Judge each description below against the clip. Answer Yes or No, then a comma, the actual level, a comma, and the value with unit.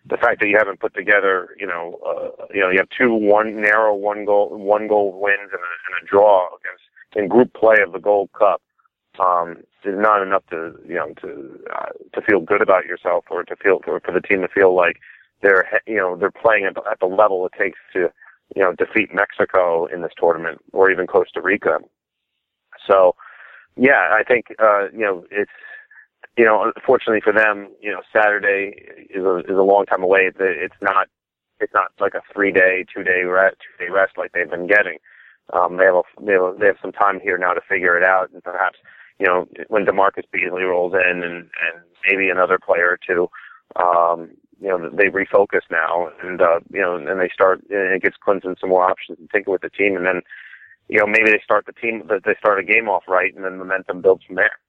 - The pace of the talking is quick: Yes, fast, 215 wpm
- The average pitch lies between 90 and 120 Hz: Yes, low, 100 Hz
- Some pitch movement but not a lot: No, wide, 6.9 semitones